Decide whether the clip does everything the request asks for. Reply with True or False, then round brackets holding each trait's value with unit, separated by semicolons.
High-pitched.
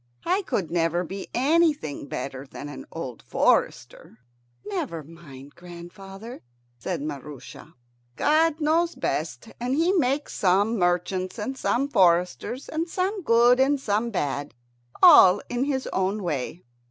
True (195 Hz)